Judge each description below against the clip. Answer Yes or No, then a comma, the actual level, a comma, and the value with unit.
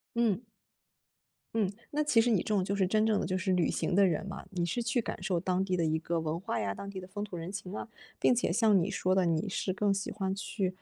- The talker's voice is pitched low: No, high, 195 Hz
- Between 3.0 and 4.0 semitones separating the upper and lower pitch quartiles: No, narrow, 2.6 semitones